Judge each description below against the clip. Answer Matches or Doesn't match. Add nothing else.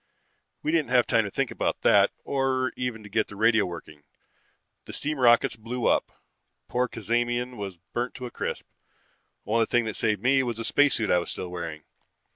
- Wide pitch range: Doesn't match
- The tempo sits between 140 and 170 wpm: Doesn't match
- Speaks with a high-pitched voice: Doesn't match